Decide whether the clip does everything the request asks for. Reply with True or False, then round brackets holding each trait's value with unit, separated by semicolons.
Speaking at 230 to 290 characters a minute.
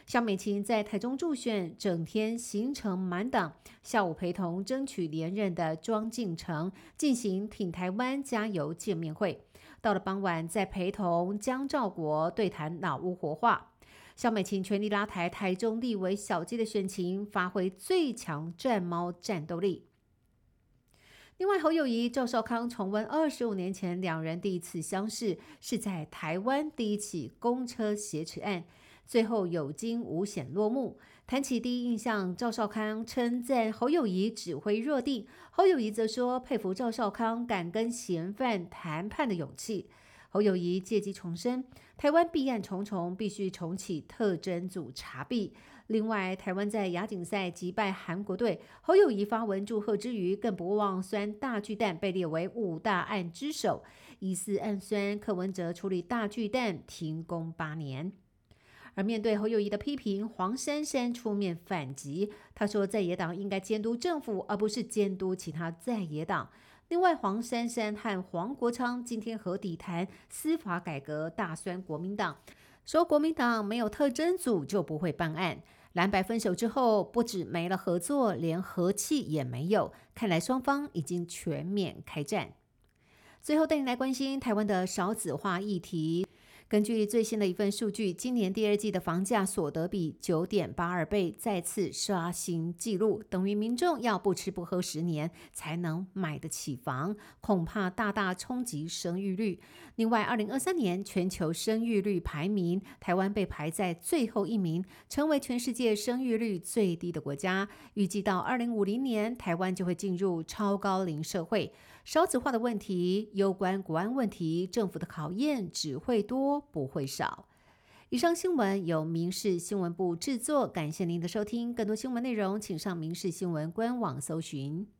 True (250 characters per minute)